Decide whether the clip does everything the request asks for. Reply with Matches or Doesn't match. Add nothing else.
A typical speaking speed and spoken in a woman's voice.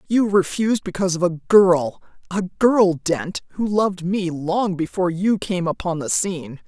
Matches